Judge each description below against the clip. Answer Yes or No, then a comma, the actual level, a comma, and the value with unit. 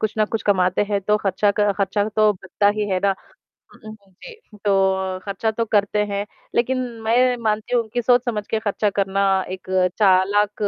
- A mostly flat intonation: Yes, narrow, 2.1 semitones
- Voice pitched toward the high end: Yes, high, 205 Hz